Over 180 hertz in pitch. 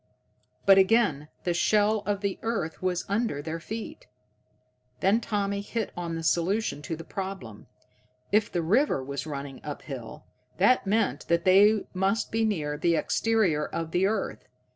Yes: high, 190 Hz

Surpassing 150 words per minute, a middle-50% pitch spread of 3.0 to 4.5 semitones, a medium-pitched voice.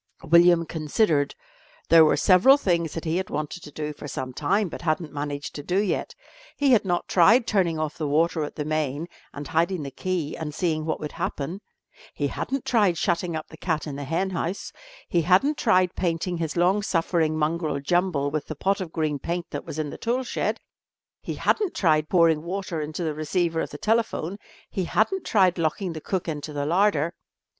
Yes: average, 200 wpm; average, 3.3 semitones; medium, 165 Hz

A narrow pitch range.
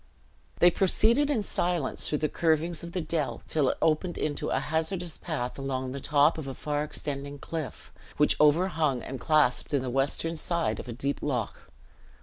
No: average, 3.5 semitones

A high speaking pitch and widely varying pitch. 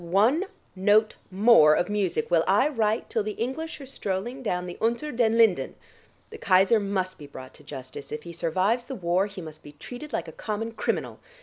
No: high, 200 Hz; average, 5.0 semitones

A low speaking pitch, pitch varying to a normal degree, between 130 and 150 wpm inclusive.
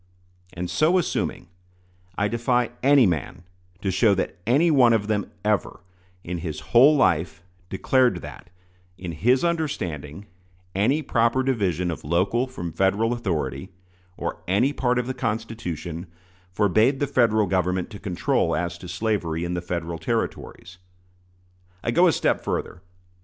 No: low, 100 Hz; wide, 5.7 semitones; average, 145 wpm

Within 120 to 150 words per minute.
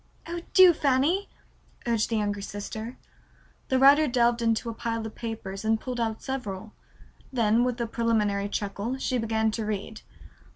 No: average, 160 wpm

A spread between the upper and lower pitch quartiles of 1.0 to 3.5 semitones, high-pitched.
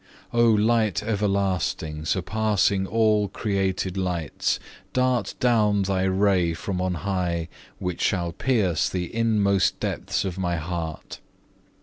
No: average, 3.1 semitones; very low, 95 Hz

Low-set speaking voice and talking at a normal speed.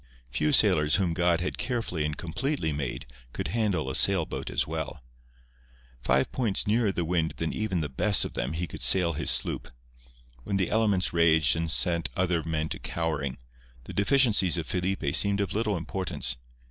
Yes: very low, 85 Hz; average, 175 wpm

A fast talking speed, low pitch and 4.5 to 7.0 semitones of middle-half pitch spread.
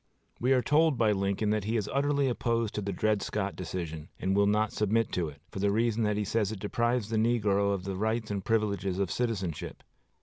No: fast, 225 wpm; low, 105 Hz; average, 2.8 semitones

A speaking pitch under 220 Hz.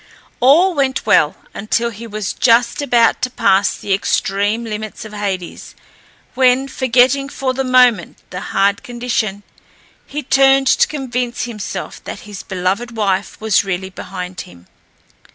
No: high, 230 Hz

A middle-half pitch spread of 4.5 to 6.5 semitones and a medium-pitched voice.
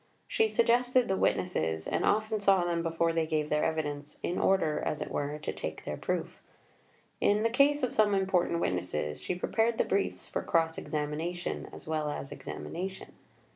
Yes: wide, 5.4 semitones; medium, 170 Hz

